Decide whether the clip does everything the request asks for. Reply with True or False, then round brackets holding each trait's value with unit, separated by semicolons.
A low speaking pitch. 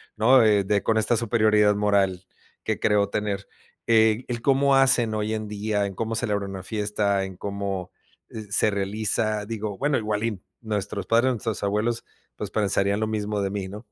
True (105 Hz)